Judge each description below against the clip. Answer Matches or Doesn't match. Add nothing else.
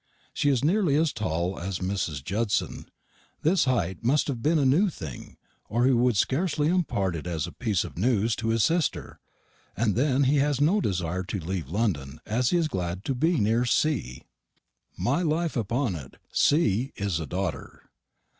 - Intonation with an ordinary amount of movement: Doesn't match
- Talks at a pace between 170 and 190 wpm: Matches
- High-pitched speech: Doesn't match